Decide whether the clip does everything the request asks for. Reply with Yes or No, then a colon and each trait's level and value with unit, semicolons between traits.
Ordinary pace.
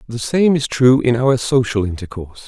Yes: average, 195 wpm